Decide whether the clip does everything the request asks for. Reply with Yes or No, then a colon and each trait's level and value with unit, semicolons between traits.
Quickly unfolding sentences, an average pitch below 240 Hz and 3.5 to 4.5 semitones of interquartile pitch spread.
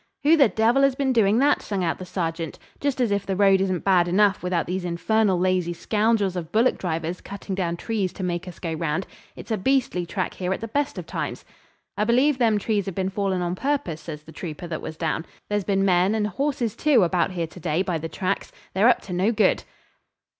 Yes: fast, 230 wpm; high, 190 Hz; average, 4.0 semitones